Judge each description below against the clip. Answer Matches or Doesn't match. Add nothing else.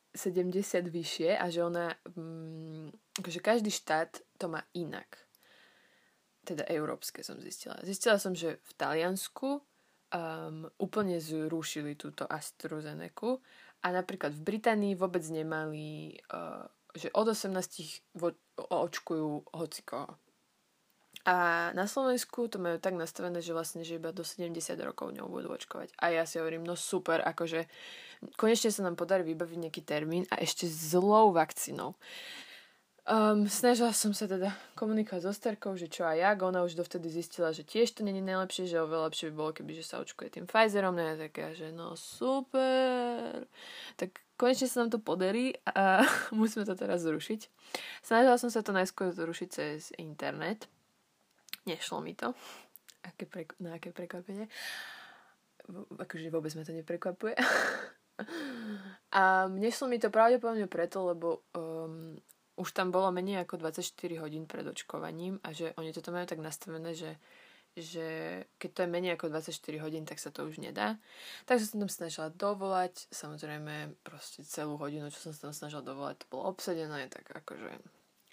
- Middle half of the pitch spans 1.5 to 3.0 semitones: Doesn't match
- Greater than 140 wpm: Matches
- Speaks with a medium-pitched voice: Matches